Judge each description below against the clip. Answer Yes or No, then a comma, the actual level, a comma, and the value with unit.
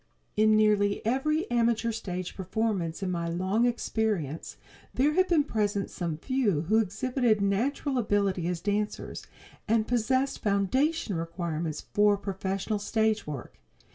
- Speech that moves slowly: Yes, slow, 130 wpm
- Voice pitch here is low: No, high, 210 Hz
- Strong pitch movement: No, average, 3.9 semitones